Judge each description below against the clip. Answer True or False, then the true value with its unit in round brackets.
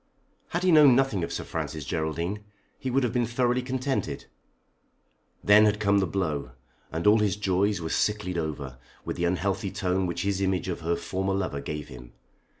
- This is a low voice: True (95 Hz)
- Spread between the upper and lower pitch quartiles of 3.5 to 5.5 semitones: True (4.1 semitones)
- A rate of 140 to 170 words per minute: False (185 wpm)